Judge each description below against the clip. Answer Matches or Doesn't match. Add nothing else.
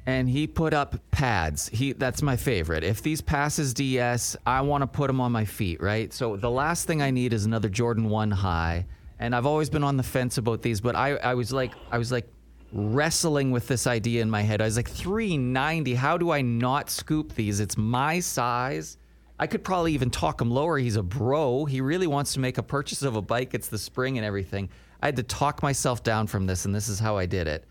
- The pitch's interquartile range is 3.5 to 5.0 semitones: Matches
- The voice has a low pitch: Matches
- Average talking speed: Doesn't match